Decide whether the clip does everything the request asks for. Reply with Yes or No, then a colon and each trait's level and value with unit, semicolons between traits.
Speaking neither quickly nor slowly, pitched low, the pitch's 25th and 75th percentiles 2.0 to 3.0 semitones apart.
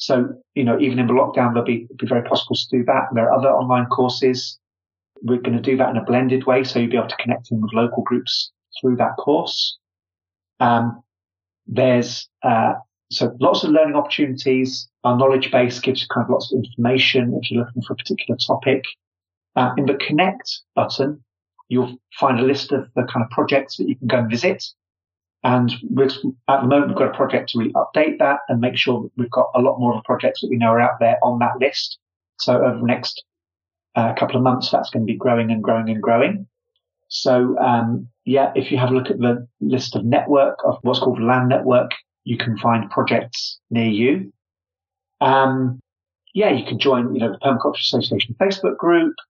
No: fast, 210 wpm; low, 125 Hz; narrow, 2.5 semitones